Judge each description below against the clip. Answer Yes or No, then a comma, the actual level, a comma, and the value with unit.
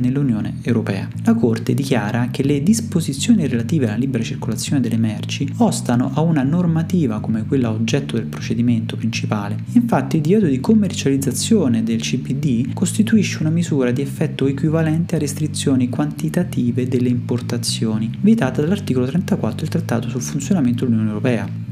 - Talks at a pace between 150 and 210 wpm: No, average, 140 wpm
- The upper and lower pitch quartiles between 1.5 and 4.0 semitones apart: No, average, 5.1 semitones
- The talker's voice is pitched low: Yes, low, 130 Hz